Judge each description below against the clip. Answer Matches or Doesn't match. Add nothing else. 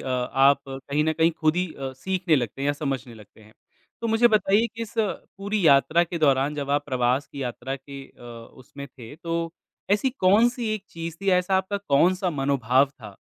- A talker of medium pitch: Matches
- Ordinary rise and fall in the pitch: Doesn't match